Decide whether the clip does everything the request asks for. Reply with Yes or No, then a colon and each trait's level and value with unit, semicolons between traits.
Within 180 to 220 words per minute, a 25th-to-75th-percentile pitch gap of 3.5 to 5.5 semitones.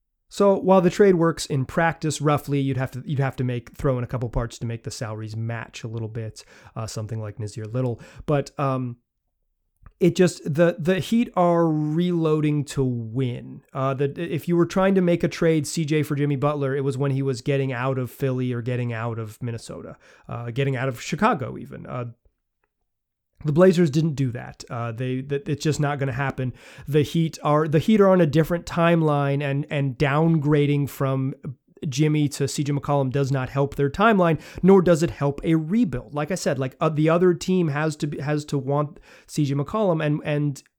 Yes: fast, 205 wpm; average, 4.1 semitones